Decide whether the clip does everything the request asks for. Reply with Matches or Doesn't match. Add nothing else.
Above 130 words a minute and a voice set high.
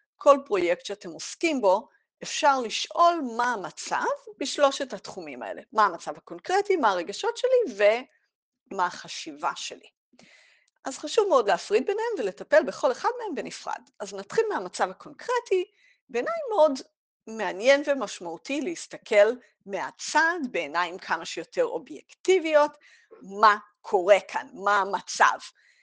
Doesn't match